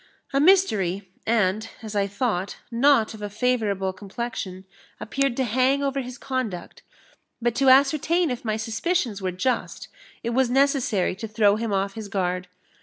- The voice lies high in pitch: Yes, high, 225 Hz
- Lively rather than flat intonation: No, average, 4.7 semitones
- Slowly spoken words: No, average, 160 wpm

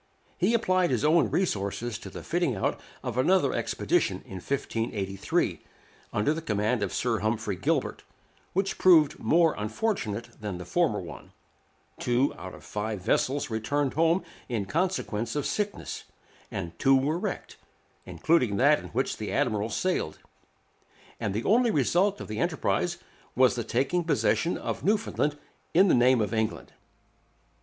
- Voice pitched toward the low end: Yes, low, 130 Hz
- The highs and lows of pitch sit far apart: Yes, wide, 7.6 semitones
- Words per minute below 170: Yes, average, 150 wpm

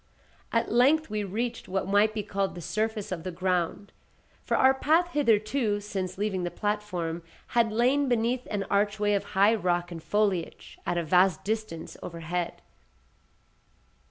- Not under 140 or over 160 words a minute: Yes, average, 155 wpm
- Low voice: No, high, 205 Hz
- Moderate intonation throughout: Yes, average, 3.6 semitones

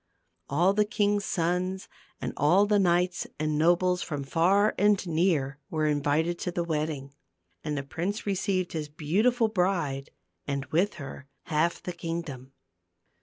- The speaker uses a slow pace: No, average, 145 wpm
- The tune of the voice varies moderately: Yes, average, 4.1 semitones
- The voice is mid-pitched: Yes, medium, 170 Hz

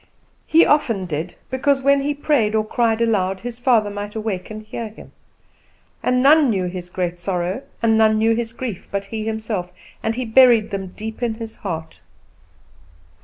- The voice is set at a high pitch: Yes, high, 220 Hz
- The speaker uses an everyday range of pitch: Yes, average, 3.7 semitones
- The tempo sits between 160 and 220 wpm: Yes, average, 175 wpm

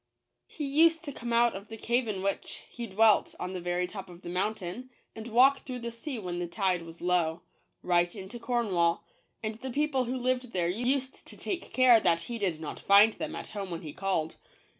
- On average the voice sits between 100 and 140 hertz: No, high, 215 Hz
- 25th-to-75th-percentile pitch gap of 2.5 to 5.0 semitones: No, wide, 5.5 semitones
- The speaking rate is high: Yes, fast, 215 wpm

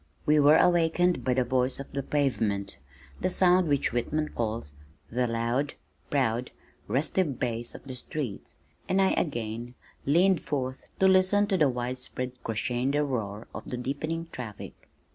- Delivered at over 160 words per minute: No, average, 150 wpm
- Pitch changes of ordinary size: Yes, average, 4.5 semitones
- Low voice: Yes, low, 130 Hz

